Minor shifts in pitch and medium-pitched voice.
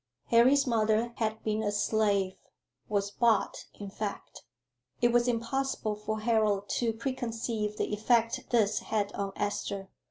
No: narrow, 2.2 semitones; high, 220 Hz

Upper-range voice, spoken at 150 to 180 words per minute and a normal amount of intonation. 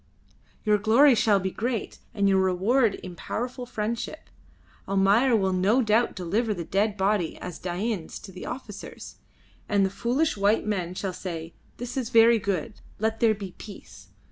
Yes: high, 210 Hz; average, 165 wpm; average, 3.4 semitones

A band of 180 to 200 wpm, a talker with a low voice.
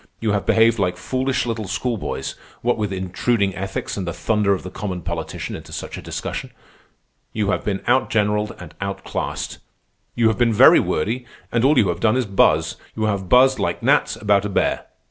Yes: average, 190 wpm; low, 105 Hz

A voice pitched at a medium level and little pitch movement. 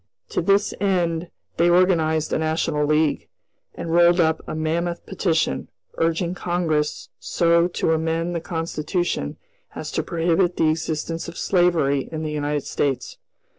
Yes: medium, 165 Hz; narrow, 1.7 semitones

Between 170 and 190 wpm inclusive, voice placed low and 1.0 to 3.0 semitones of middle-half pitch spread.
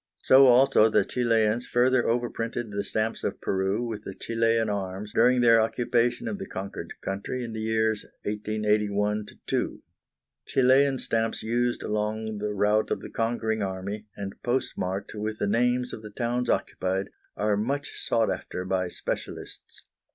No: average, 150 wpm; low, 110 Hz; average, 2.7 semitones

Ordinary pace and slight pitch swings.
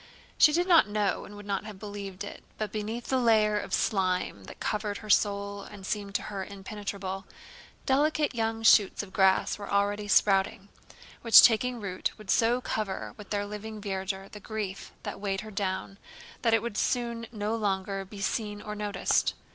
Yes: average, 180 wpm; narrow, 2.0 semitones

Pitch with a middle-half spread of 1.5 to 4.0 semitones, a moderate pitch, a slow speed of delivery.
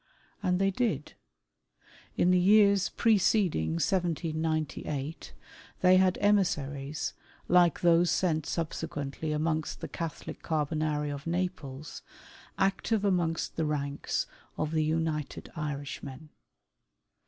Yes: average, 3.5 semitones; medium, 160 Hz; slow, 100 wpm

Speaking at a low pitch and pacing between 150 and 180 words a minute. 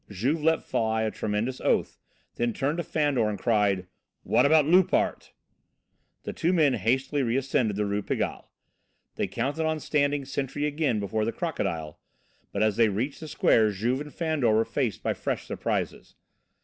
Yes: low, 125 Hz; average, 165 wpm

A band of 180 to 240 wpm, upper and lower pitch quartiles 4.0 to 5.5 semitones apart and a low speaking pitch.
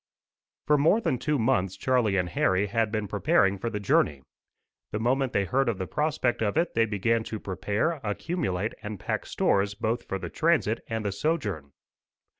Yes: average, 185 wpm; average, 5.1 semitones; low, 110 Hz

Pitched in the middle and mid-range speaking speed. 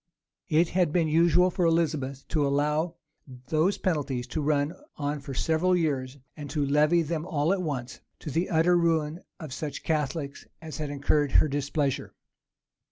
Yes: medium, 150 Hz; average, 165 wpm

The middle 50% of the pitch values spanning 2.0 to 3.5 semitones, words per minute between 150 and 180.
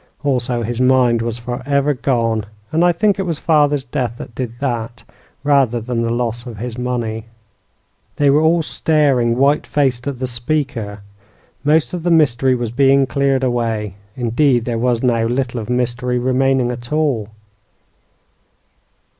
Yes: average, 3.0 semitones; average, 155 wpm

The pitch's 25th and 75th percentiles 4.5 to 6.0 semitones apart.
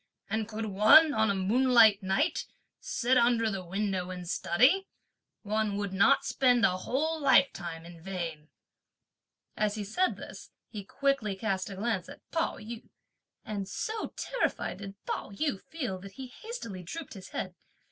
Yes: average, 4.8 semitones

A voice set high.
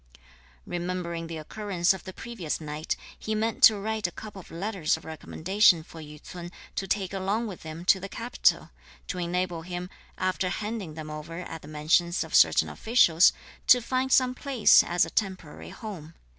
No: medium, 180 Hz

